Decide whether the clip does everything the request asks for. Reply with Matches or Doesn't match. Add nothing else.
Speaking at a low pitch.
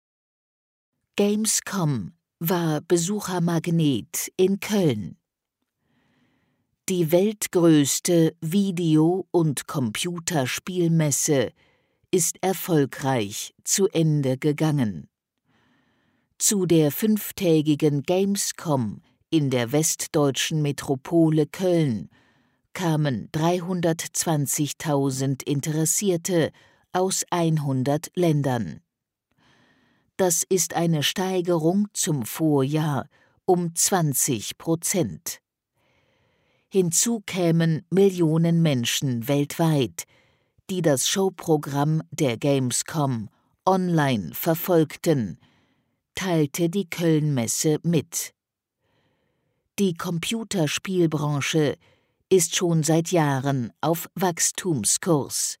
Doesn't match